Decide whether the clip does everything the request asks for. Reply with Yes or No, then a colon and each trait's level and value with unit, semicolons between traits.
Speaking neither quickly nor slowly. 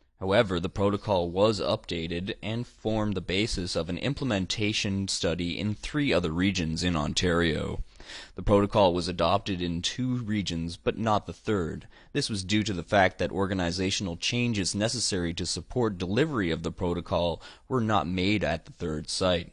Yes: average, 165 wpm